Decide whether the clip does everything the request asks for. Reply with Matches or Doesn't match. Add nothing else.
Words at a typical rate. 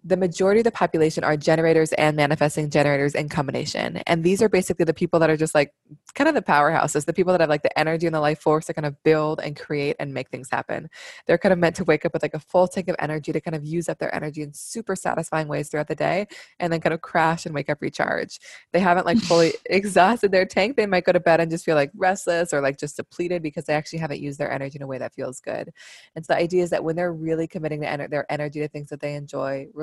Doesn't match